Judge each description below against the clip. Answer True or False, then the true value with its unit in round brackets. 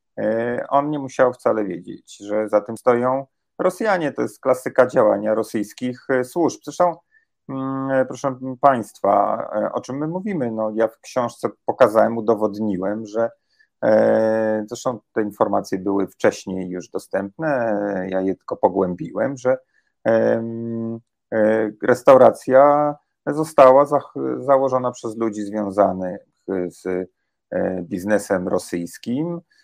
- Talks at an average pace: False (105 wpm)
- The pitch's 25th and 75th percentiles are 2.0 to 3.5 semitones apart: False (4.3 semitones)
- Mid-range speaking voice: False (115 Hz)